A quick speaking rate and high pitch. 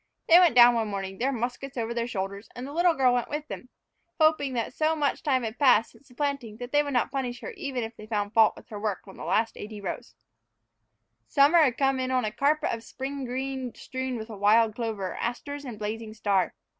Yes: fast, 230 wpm; high, 245 Hz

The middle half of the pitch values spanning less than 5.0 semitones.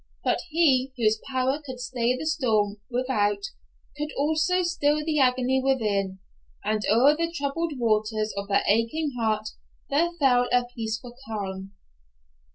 No: average, 5.3 semitones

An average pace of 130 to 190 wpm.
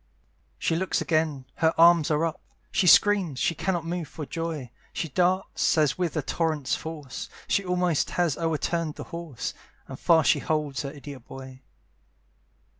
Yes: average, 160 wpm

